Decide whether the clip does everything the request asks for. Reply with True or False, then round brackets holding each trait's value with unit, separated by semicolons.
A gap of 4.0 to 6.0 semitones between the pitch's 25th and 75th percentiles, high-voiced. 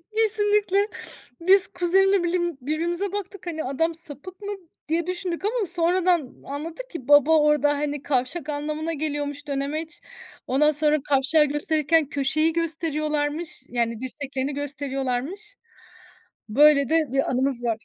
False (3.5 semitones; 310 Hz)